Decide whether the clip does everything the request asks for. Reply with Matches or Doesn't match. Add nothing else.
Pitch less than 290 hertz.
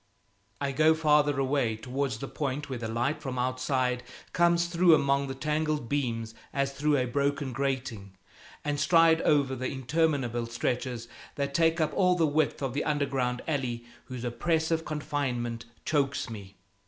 Matches